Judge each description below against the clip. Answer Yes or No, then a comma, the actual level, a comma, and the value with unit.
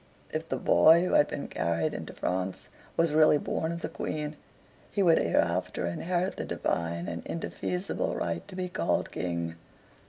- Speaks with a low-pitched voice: No, medium, 150 Hz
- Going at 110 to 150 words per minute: No, average, 165 wpm